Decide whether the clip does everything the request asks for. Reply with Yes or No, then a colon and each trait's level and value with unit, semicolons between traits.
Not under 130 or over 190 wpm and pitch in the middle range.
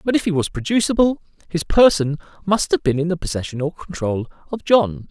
No: average, 200 wpm; medium, 170 Hz